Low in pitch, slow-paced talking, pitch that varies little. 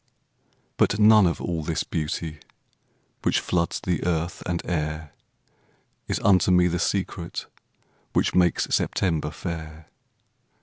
Yes: very low, 85 Hz; slow, 120 wpm; narrow, 2.3 semitones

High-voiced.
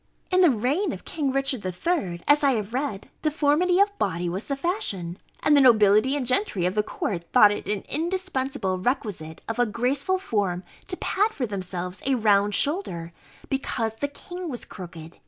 Yes: high, 245 Hz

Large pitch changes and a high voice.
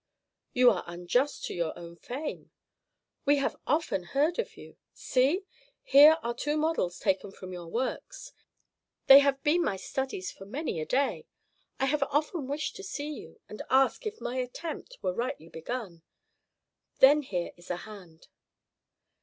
Yes: wide, 7.9 semitones; very high, 260 Hz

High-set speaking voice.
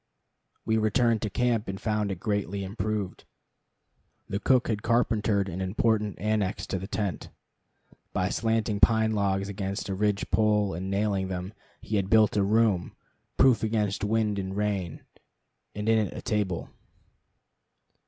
No: low, 105 Hz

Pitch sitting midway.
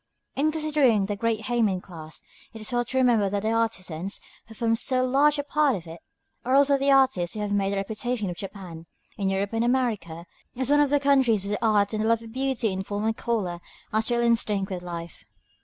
No: high, 220 Hz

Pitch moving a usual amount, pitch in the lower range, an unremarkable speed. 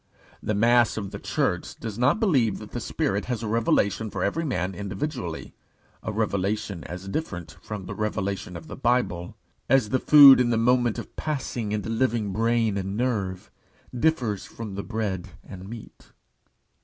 Yes: average, 3.7 semitones; low, 110 Hz; average, 170 wpm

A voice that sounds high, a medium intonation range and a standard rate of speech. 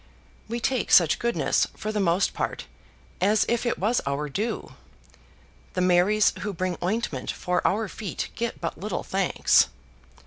Yes: high, 200 Hz; average, 3.7 semitones; average, 150 wpm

